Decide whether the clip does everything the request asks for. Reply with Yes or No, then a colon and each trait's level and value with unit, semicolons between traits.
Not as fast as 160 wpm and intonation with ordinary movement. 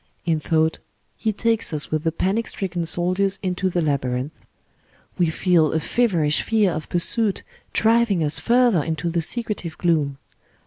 Yes: average, 150 wpm; average, 4.5 semitones